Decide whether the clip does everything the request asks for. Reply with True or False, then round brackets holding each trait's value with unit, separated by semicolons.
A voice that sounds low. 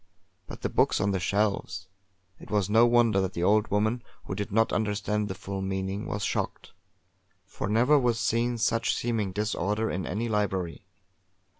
True (105 Hz)